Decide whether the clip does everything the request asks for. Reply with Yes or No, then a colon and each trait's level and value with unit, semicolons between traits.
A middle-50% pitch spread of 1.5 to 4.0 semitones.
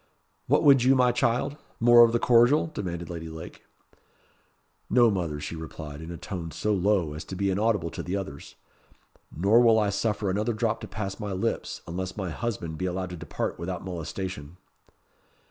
No: average, 5.2 semitones